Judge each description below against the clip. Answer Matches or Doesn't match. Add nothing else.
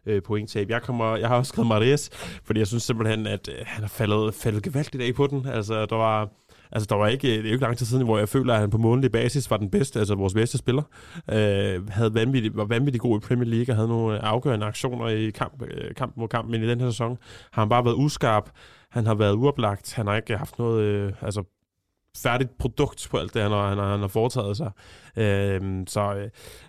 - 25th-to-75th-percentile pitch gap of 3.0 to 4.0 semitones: Doesn't match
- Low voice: Matches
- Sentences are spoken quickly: Matches